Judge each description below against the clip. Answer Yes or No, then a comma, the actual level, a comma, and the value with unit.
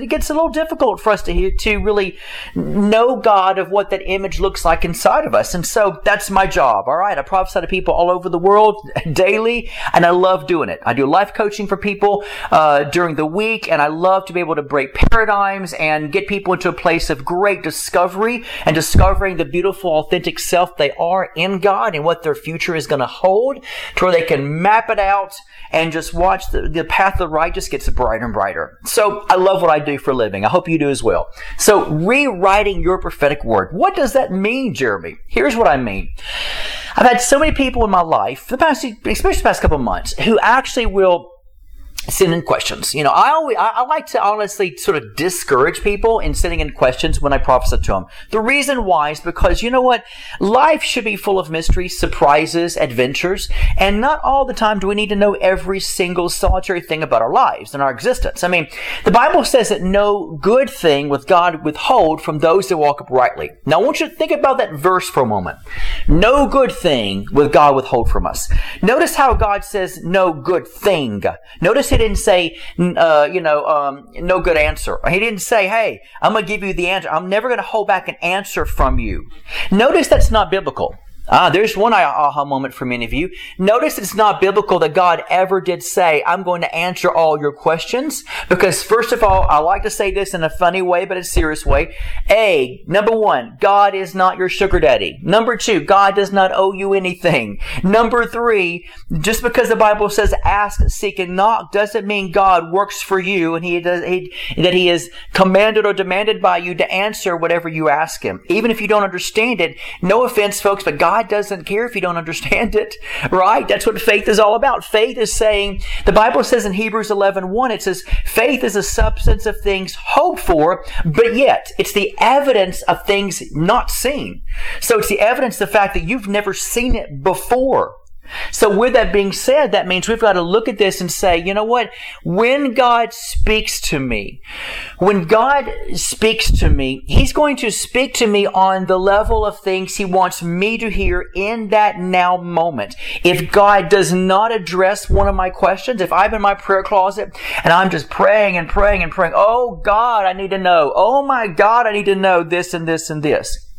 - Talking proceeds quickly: Yes, fast, 215 wpm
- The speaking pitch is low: No, high, 195 Hz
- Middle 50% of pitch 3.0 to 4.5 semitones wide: Yes, average, 3.9 semitones